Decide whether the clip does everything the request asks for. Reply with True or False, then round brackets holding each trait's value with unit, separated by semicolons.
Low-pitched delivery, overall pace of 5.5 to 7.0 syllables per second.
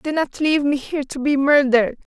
False (280 Hz; 6.1 syllables/s)